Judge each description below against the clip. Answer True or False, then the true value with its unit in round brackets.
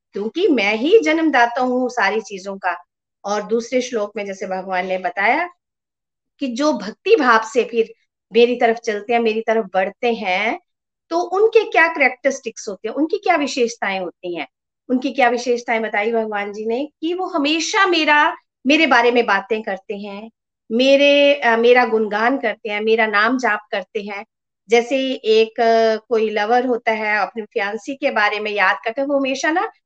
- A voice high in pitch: True (235 Hz)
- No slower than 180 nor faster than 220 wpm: False (170 wpm)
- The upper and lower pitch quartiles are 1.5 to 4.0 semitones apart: False (4.6 semitones)